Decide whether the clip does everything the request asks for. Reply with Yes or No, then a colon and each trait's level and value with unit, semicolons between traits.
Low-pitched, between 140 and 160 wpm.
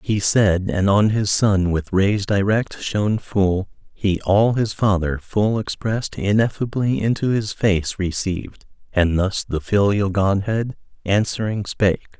Yes: low, 100 Hz; average, 145 wpm